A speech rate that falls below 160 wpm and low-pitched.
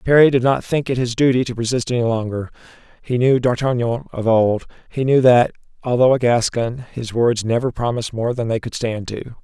No: fast, 205 wpm; low, 120 Hz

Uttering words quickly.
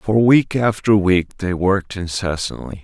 No: average, 150 wpm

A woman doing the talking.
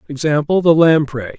No: male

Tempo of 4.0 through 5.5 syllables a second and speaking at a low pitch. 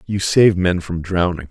Yes: 5.0 syllables/s; very low, 90 Hz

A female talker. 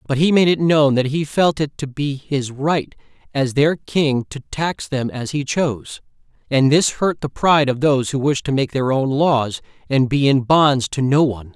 No: male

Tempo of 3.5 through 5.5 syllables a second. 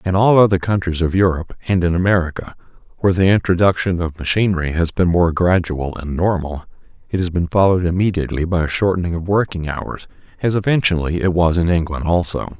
No: 6.1 syllables/s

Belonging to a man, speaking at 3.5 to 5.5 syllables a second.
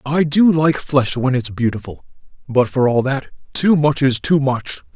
Yes: male; 4.5 syllables/s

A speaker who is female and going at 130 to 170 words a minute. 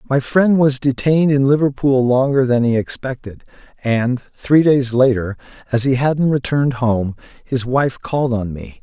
No: male; average, 165 wpm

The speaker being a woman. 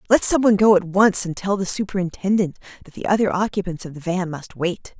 Yes: female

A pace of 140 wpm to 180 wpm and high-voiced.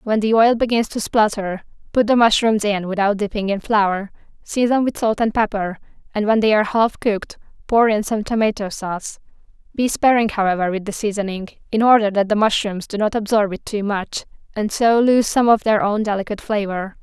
No: average, 195 wpm; high, 210 Hz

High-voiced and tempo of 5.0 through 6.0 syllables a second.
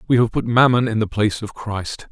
No: low, 110 Hz; 5.7 syllables/s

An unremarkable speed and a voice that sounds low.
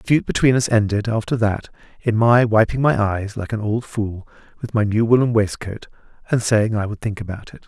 No: fast, 220 wpm; low, 110 Hz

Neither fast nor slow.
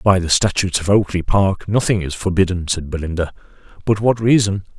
Yes: average, 175 wpm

